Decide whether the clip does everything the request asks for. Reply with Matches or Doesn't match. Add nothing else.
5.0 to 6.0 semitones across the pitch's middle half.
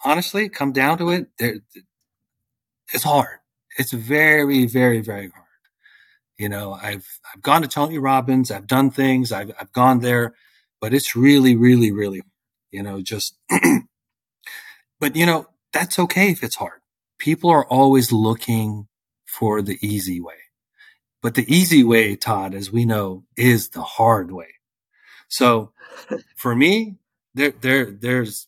Doesn't match